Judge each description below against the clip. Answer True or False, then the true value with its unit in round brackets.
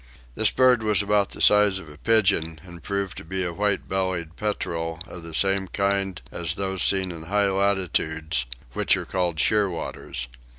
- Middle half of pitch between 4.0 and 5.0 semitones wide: False (3.3 semitones)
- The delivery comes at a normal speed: True (175 wpm)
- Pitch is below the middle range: True (95 Hz)